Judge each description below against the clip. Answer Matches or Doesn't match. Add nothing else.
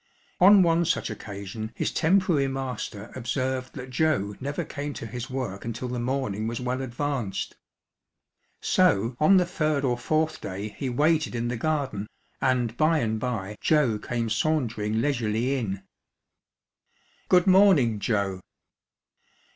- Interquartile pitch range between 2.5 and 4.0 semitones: Doesn't match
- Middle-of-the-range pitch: Doesn't match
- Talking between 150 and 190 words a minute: Doesn't match